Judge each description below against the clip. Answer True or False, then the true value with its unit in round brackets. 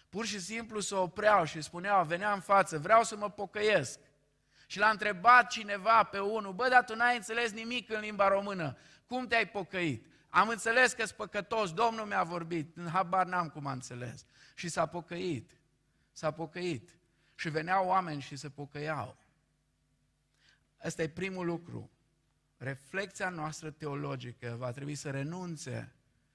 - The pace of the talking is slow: False (155 wpm)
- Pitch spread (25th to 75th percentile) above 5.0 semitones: True (5.5 semitones)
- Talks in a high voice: False (180 Hz)